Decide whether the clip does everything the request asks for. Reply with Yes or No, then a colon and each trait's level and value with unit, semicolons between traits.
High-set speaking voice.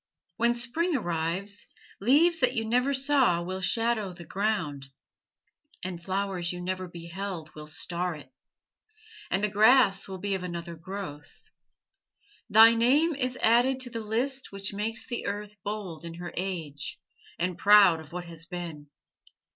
Yes: high, 195 Hz